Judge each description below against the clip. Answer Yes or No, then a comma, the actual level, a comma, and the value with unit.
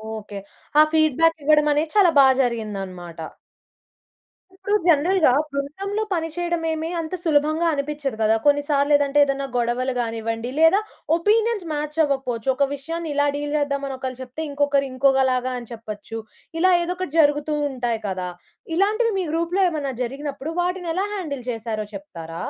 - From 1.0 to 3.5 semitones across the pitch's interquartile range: No, average, 4.7 semitones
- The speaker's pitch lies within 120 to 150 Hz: No, very high, 285 Hz